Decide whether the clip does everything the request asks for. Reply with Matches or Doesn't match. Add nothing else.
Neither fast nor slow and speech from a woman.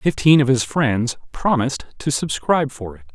Doesn't match